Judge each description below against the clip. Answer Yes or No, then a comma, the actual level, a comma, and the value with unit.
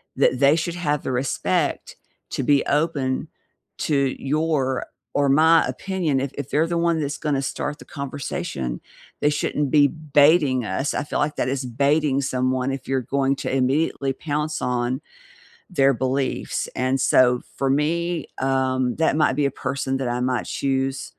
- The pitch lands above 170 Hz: No, medium, 140 Hz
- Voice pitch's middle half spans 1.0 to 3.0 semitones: Yes, narrow, 2.4 semitones